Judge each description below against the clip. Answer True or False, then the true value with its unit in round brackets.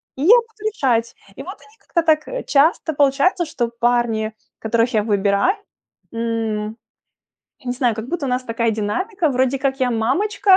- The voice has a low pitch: False (255 Hz)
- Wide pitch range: True (6.7 semitones)